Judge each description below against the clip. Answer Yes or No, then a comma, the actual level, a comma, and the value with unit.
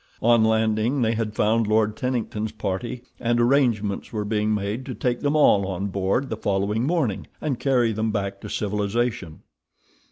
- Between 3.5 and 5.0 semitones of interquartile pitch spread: No, average, 2.7 semitones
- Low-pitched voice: Yes, low, 110 Hz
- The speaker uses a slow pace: No, average, 165 wpm